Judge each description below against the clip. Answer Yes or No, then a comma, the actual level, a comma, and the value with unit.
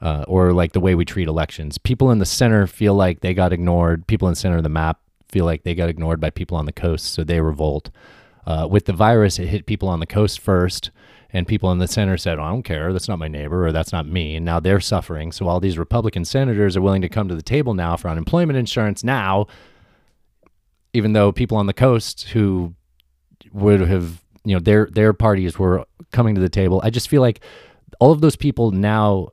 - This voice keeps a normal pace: No, fast, 235 wpm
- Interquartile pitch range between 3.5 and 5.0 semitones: Yes, average, 3.9 semitones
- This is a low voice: Yes, very low, 95 Hz